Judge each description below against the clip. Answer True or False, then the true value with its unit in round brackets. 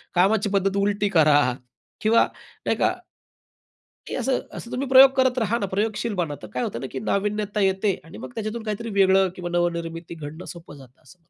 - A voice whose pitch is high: True (195 Hz)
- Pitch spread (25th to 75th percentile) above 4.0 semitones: True (4.4 semitones)